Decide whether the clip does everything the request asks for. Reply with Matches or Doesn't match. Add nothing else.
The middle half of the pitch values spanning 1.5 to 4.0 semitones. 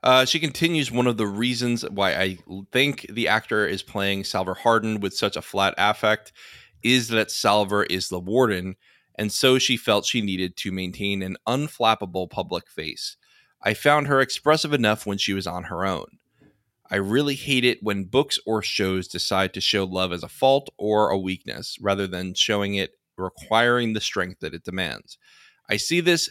Doesn't match